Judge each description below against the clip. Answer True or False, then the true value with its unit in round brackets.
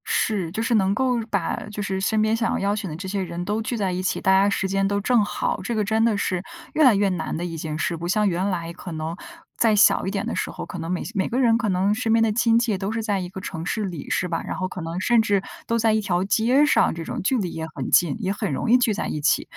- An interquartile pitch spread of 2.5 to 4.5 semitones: True (3.6 semitones)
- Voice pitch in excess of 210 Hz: False (200 Hz)